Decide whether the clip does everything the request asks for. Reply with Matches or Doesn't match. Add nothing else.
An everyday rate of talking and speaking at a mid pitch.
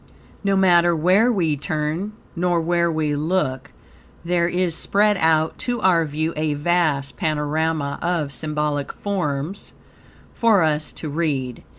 Doesn't match